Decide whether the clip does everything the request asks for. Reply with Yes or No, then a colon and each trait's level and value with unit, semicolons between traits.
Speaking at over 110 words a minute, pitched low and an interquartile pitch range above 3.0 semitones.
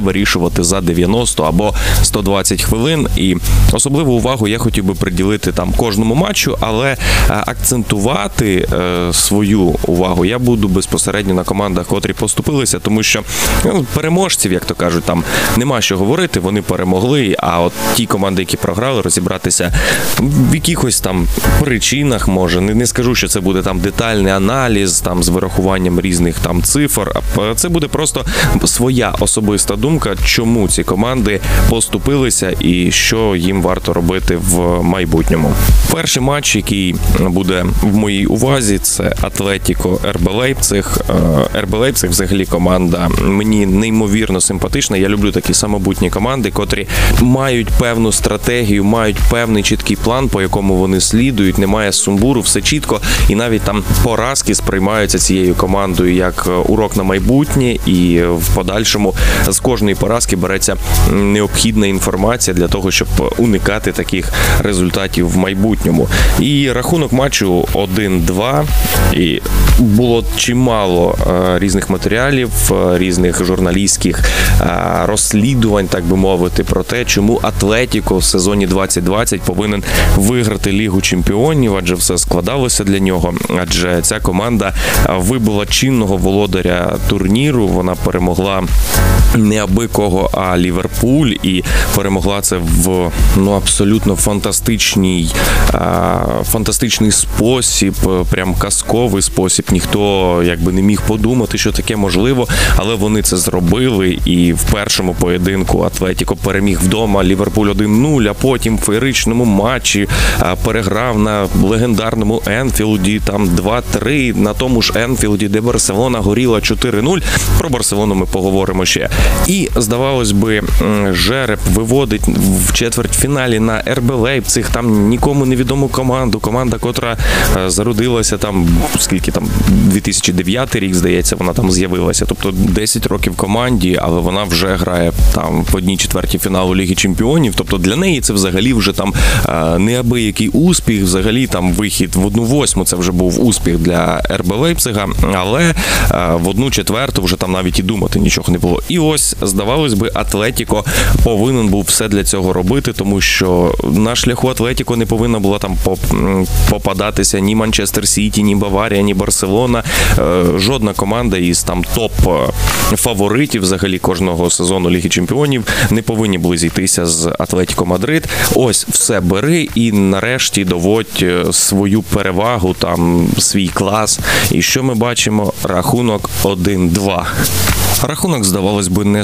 Yes: average, 130 wpm; low, 100 Hz; average, 3.6 semitones